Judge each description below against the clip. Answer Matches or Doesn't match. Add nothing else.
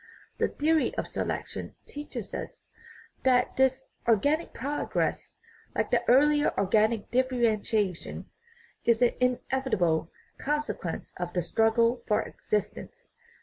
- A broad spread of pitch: Doesn't match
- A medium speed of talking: Doesn't match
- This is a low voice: Doesn't match